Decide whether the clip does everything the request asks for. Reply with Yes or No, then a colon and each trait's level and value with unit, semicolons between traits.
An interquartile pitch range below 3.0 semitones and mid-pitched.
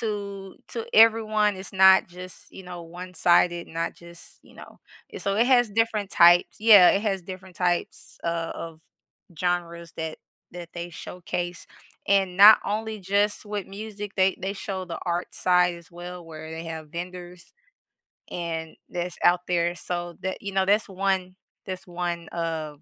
Yes: narrow, 2.4 semitones; medium, 180 Hz